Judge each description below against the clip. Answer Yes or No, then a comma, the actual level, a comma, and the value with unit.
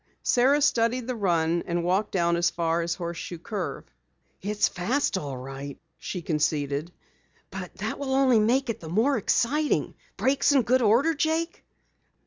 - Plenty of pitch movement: Yes, wide, 7.4 semitones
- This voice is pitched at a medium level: No, high, 205 Hz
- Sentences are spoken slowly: No, average, 155 wpm